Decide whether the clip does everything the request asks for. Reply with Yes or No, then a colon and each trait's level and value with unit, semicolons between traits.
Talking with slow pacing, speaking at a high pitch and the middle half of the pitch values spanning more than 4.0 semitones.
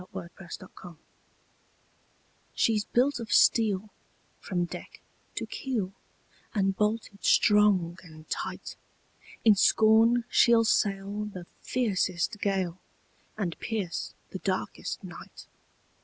No: slow, 110 wpm; high, 200 Hz; average, 3.1 semitones